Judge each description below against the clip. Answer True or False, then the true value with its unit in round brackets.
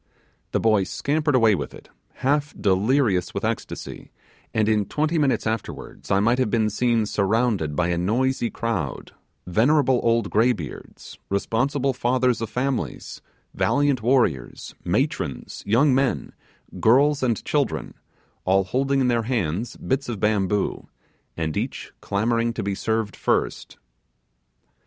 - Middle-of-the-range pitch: False (115 Hz)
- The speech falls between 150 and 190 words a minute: False (135 wpm)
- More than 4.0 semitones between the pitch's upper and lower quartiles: True (4.4 semitones)